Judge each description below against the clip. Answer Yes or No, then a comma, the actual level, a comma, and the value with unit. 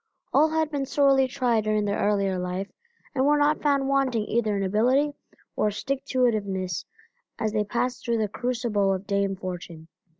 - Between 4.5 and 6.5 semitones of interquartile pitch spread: Yes, average, 5.3 semitones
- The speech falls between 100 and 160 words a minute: No, average, 185 wpm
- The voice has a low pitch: No, high, 220 Hz